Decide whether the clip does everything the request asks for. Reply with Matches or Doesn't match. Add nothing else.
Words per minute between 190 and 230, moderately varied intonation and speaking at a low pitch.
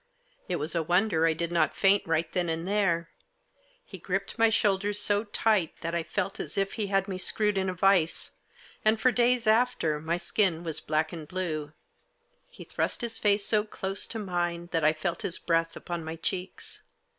Doesn't match